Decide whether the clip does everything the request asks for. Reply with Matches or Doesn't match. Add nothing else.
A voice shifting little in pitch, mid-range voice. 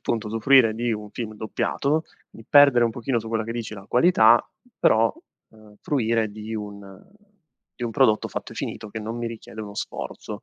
Doesn't match